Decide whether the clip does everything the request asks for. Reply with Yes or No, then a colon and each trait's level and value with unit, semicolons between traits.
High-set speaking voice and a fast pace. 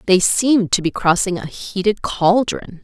No: high, 195 Hz; average, 170 wpm